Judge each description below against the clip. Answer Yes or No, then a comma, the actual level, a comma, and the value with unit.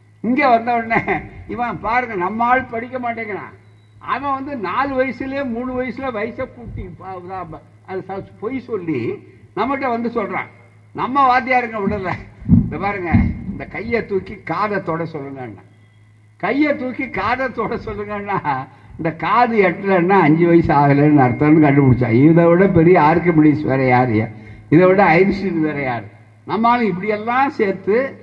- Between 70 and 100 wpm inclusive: No, fast, 130 wpm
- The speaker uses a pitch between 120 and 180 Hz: No, high, 190 Hz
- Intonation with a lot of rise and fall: Yes, wide, 8.7 semitones